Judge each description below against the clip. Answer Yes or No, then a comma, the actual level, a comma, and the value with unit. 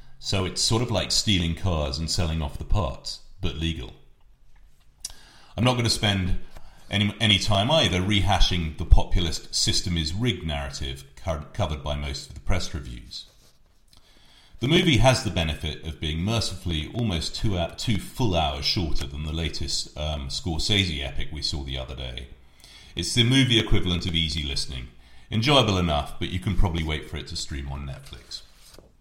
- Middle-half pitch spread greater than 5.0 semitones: Yes, wide, 5.5 semitones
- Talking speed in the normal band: Yes, average, 170 wpm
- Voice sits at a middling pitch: No, very low, 85 Hz